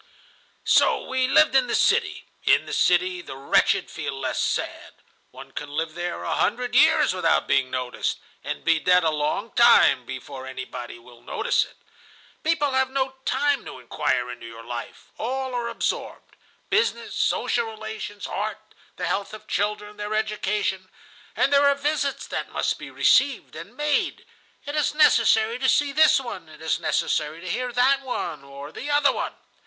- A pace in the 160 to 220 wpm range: Yes, average, 170 wpm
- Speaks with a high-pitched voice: Yes, high, 220 Hz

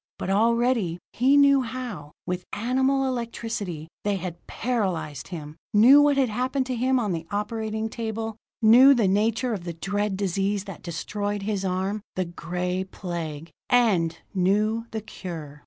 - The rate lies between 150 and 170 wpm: Yes, average, 155 wpm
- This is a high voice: Yes, high, 205 Hz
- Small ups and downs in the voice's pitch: No, average, 4.5 semitones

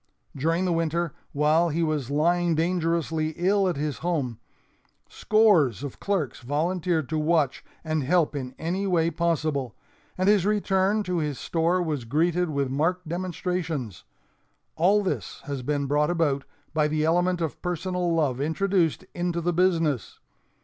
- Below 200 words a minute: Yes, average, 150 wpm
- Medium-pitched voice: Yes, medium, 165 Hz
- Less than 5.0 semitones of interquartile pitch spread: Yes, average, 3.1 semitones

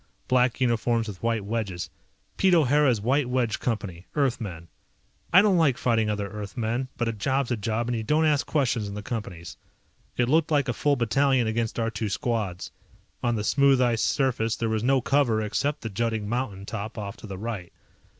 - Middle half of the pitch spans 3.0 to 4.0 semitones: Yes, average, 3.7 semitones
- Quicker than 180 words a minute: Yes, average, 190 wpm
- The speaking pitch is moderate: No, low, 115 Hz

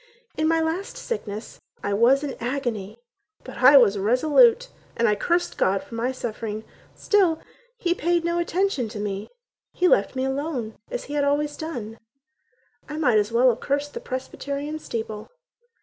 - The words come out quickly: No, average, 165 wpm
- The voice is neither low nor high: No, very high, 265 Hz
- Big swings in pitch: Yes, wide, 6.2 semitones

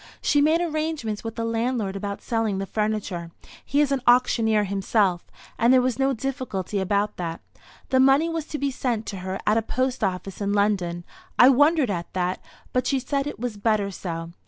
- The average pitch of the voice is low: No, high, 225 Hz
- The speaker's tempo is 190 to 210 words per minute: Yes, average, 195 wpm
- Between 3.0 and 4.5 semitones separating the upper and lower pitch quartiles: No, average, 5.0 semitones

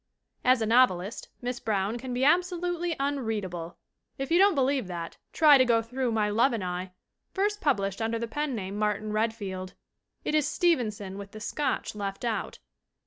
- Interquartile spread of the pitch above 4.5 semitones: Yes, wide, 5.5 semitones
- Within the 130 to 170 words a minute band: No, average, 180 wpm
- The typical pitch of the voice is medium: No, high, 230 Hz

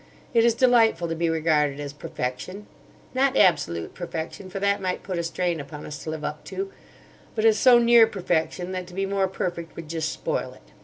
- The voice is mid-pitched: Yes, medium, 175 Hz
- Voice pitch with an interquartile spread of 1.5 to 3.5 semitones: No, average, 4.3 semitones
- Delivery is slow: No, average, 200 wpm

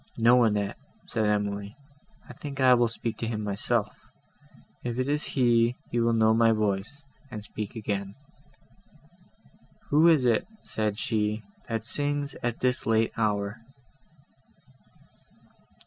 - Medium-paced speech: No, slow, 125 wpm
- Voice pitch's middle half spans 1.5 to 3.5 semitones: Yes, average, 2.8 semitones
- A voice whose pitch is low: Yes, low, 115 Hz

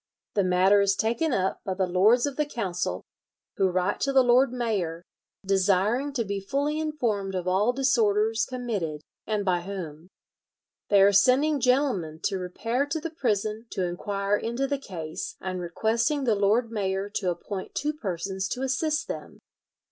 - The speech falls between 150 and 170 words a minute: Yes, average, 165 wpm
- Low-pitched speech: No, high, 205 Hz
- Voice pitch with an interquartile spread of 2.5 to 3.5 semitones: No, average, 5.1 semitones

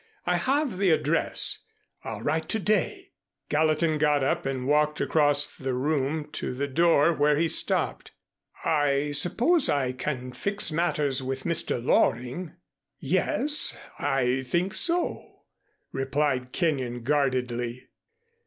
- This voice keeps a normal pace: No, slow, 125 wpm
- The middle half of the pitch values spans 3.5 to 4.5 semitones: Yes, average, 4.0 semitones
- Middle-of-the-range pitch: Yes, medium, 145 Hz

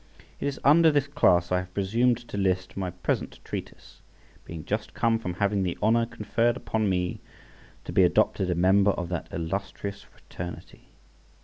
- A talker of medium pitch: No, low, 100 Hz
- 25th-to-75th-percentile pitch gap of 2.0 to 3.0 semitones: No, average, 4.3 semitones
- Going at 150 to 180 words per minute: Yes, average, 170 wpm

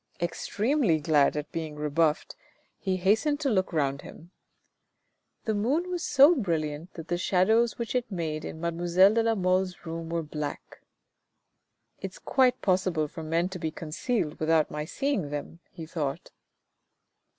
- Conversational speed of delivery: Yes, average, 155 wpm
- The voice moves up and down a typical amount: No, wide, 5.8 semitones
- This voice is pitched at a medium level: Yes, medium, 175 Hz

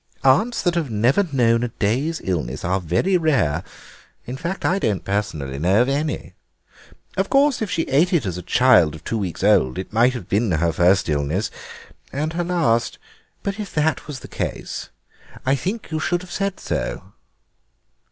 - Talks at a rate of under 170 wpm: No, average, 180 wpm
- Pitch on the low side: Yes, low, 125 Hz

